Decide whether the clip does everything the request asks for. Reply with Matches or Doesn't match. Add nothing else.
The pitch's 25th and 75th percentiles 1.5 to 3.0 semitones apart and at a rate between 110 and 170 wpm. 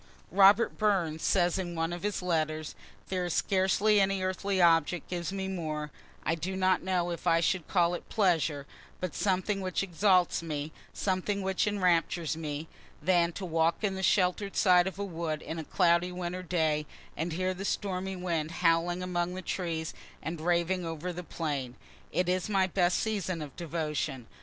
Doesn't match